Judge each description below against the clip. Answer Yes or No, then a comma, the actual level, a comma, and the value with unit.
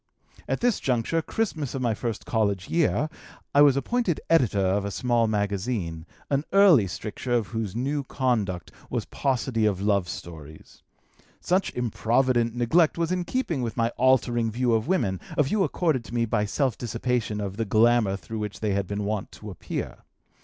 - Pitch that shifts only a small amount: No, average, 4.9 semitones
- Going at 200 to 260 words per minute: No, average, 175 wpm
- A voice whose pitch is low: Yes, low, 115 Hz